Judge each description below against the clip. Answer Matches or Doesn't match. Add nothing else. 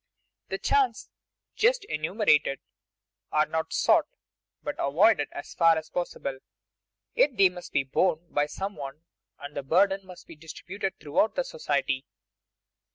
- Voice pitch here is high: Doesn't match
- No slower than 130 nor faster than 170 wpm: Matches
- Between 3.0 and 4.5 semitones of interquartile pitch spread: Doesn't match